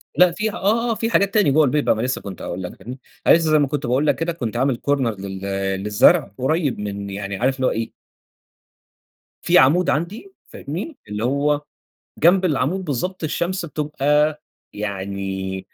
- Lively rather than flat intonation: Yes, wide, 7.6 semitones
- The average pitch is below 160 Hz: Yes, medium, 140 Hz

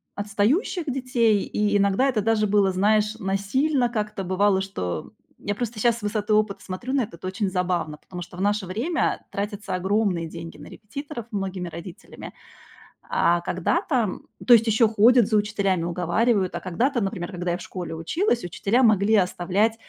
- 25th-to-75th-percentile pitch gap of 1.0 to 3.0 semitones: No, average, 3.6 semitones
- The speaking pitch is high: Yes, high, 205 Hz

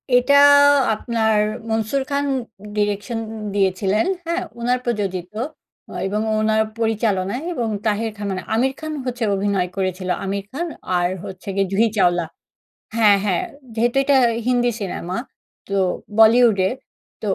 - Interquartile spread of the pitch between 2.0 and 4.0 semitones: Yes, average, 3.7 semitones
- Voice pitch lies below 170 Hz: No, high, 215 Hz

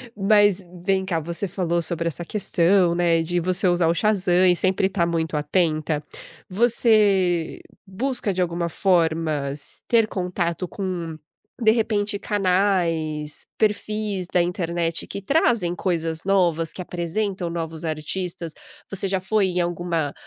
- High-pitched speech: No, medium, 180 Hz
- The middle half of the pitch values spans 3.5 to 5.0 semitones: No, average, 2.9 semitones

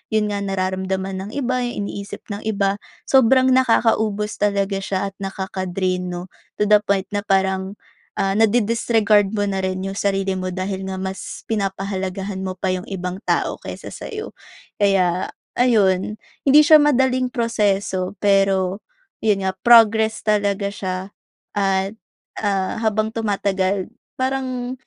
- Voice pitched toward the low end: No, high, 200 Hz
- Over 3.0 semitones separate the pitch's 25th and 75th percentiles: No, narrow, 2.6 semitones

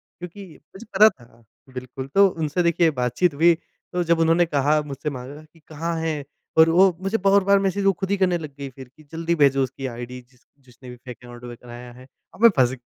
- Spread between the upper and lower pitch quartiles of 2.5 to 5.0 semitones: No, wide, 5.4 semitones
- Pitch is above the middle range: No, medium, 155 Hz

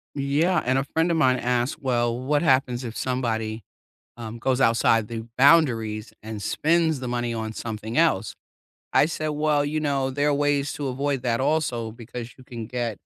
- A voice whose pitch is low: Yes, low, 130 Hz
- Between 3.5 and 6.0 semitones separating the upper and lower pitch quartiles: Yes, average, 3.9 semitones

